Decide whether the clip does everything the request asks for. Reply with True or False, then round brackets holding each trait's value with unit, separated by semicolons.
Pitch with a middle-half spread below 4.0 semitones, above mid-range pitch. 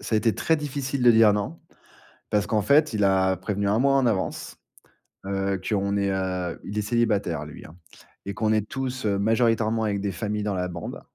False (2.8 semitones; 105 Hz)